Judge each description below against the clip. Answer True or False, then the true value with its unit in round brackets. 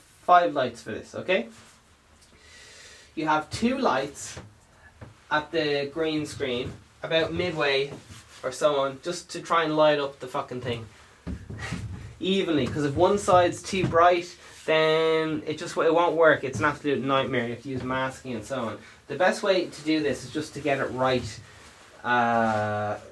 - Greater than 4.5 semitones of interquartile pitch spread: True (5.6 semitones)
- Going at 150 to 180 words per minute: True (170 wpm)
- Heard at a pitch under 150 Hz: True (140 Hz)